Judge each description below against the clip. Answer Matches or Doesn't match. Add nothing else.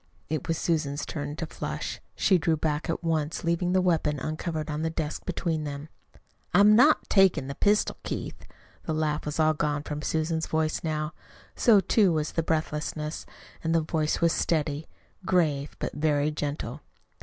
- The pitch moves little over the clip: Matches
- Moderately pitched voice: Matches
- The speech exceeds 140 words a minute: Matches